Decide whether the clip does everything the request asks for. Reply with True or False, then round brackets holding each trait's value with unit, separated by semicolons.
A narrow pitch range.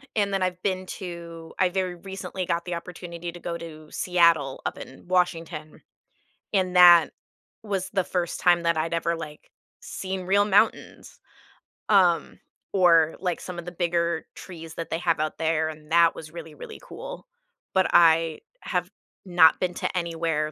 True (2.0 semitones)